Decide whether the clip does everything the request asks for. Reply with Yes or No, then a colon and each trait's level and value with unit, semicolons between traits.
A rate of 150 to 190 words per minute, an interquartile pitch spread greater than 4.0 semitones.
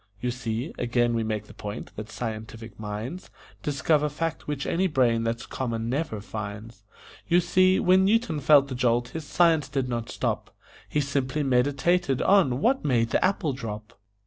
Yes: average, 170 wpm; average, 5.2 semitones